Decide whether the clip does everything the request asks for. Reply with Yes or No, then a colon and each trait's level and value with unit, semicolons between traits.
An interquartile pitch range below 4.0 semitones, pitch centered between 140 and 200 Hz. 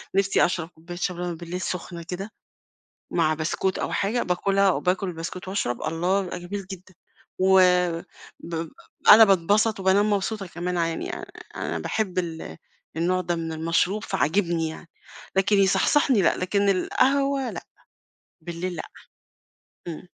Yes: average, 2.8 semitones; medium, 185 Hz